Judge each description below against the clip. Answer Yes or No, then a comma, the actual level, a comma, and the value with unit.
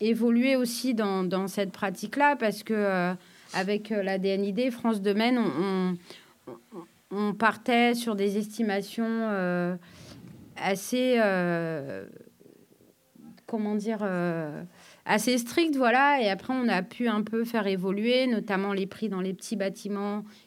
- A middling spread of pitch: Yes, average, 3.2 semitones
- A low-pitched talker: No, high, 210 Hz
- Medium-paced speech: No, slow, 135 wpm